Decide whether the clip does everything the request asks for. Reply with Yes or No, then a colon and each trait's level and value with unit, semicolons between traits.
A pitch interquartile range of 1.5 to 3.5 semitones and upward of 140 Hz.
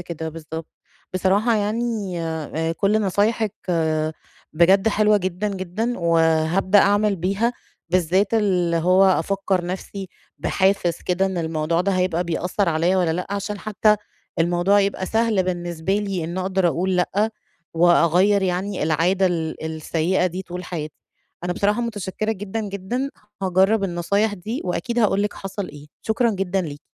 Yes: average, 3.0 semitones; medium, 185 Hz